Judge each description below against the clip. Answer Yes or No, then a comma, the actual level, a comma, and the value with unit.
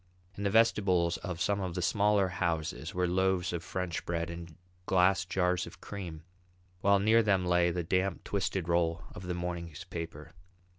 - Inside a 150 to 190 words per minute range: Yes, average, 170 wpm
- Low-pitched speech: Yes, very low, 90 Hz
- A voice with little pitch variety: Yes, narrow, 2.2 semitones